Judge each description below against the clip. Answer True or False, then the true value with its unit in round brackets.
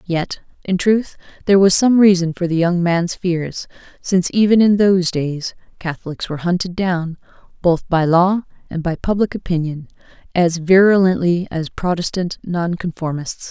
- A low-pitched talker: False (175 Hz)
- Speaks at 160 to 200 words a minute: False (145 wpm)